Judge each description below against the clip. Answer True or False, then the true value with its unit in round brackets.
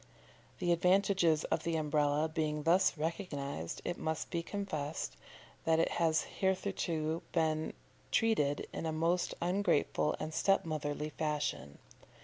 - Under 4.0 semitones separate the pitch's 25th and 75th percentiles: True (2.6 semitones)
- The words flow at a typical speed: False (125 wpm)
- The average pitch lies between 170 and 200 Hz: False (160 Hz)